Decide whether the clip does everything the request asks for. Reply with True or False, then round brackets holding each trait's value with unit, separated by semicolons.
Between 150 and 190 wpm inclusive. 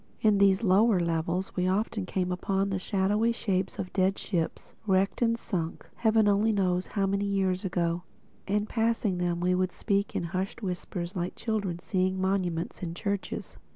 True (170 wpm)